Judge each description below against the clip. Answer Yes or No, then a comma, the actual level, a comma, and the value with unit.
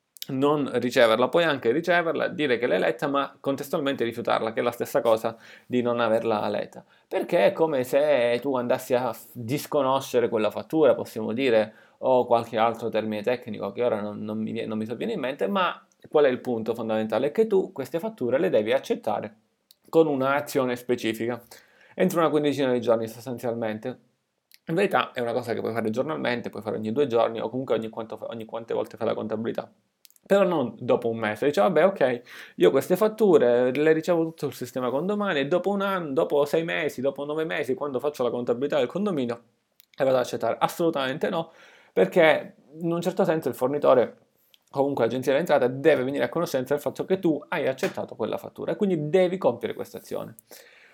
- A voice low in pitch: Yes, low, 130 Hz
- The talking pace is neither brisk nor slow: No, fast, 190 wpm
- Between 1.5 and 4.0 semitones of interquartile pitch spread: No, average, 5.0 semitones